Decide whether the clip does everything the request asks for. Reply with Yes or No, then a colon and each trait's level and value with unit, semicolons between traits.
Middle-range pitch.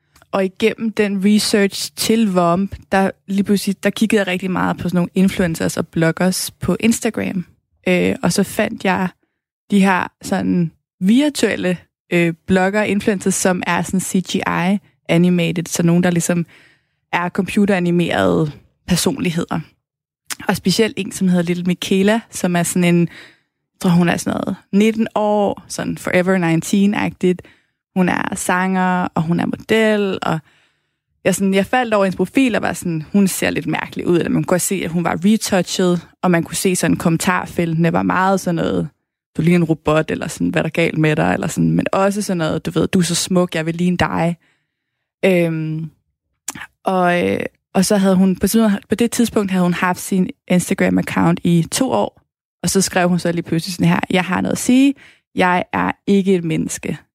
Yes: medium, 180 Hz